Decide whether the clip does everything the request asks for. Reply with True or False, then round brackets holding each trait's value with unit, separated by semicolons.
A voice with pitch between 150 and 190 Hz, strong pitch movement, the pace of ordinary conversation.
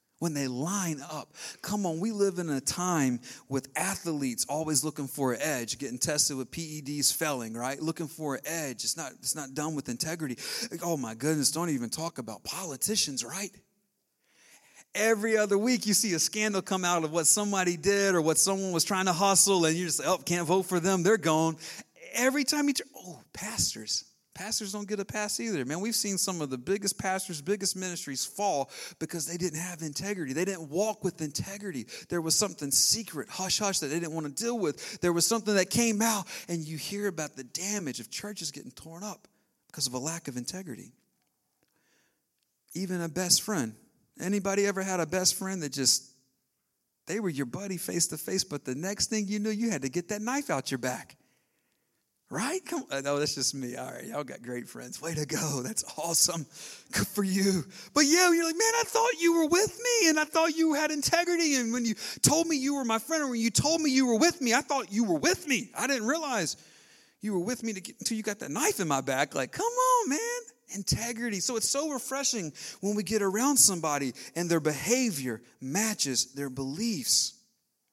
False (185 Hz; 6.2 semitones; 215 wpm)